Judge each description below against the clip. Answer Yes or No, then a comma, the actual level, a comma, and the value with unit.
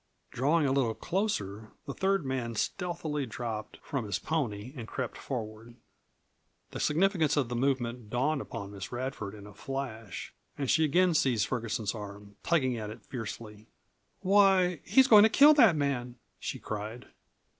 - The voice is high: No, low, 130 Hz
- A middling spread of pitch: No, wide, 6.3 semitones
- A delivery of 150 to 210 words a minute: Yes, average, 155 wpm